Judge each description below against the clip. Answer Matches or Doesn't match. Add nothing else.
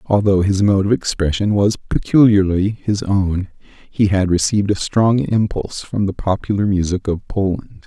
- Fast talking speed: Doesn't match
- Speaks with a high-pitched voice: Doesn't match